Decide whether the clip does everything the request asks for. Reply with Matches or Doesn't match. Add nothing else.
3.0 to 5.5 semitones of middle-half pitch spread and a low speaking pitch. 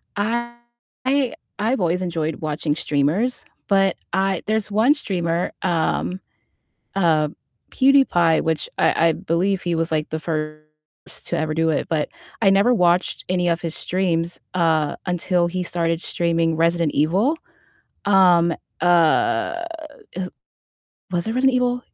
Doesn't match